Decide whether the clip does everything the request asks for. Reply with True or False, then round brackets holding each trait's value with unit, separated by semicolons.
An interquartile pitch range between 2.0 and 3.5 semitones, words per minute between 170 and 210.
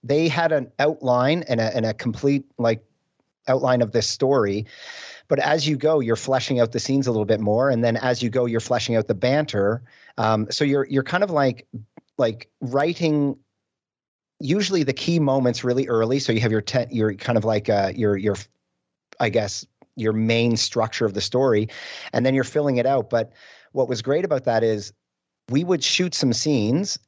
False (3.9 semitones; 200 wpm)